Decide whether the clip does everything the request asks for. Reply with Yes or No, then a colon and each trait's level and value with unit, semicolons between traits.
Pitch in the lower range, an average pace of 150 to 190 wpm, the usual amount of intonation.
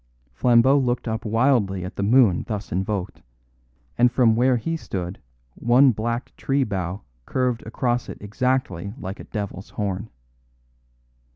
No: low, 115 Hz; slow, 135 wpm; average, 4.2 semitones